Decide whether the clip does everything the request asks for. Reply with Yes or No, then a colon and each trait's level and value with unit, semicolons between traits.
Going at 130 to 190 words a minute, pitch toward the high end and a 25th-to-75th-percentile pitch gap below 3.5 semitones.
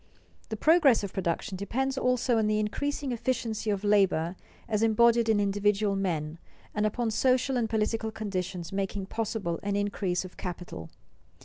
Yes: average, 150 wpm; high, 210 Hz; average, 2.9 semitones